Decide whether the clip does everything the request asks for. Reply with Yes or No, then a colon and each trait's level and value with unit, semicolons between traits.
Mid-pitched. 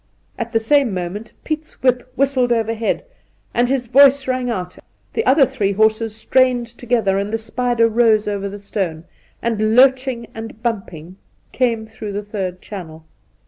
No: high, 225 Hz